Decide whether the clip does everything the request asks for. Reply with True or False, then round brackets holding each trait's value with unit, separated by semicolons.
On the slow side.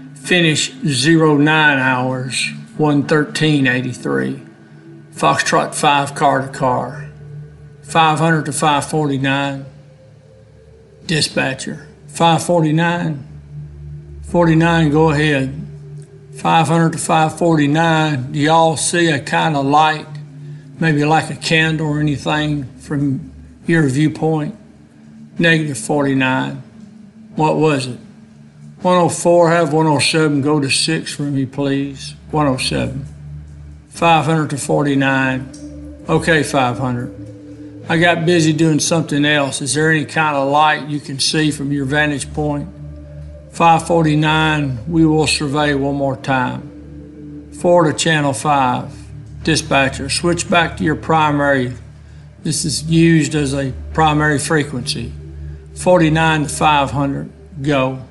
True (105 wpm)